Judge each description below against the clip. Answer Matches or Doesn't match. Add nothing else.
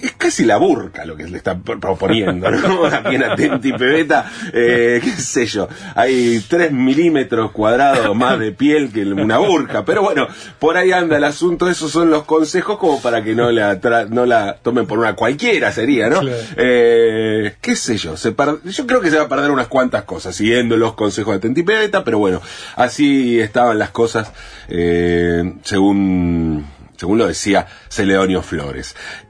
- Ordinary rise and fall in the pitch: Doesn't match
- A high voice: Doesn't match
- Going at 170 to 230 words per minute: Matches